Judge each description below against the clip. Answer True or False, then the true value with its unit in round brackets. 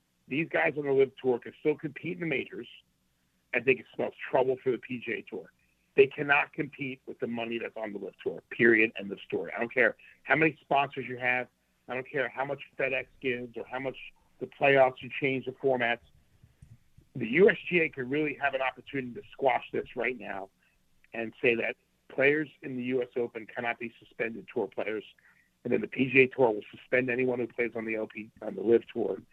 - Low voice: True (130 Hz)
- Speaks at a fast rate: True (210 wpm)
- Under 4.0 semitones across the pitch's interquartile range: True (3.3 semitones)